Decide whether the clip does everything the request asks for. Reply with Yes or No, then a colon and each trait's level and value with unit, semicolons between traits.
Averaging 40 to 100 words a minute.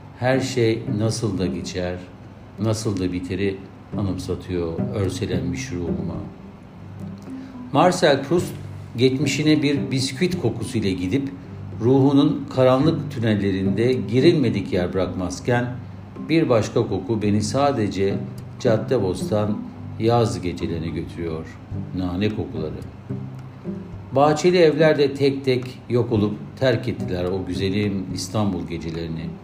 Yes: slow, 95 wpm